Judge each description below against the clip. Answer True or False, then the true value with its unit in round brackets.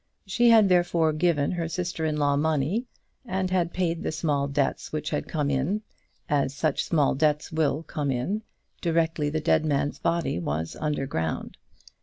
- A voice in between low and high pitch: True (155 Hz)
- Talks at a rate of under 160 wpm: False (170 wpm)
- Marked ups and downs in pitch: False (3.3 semitones)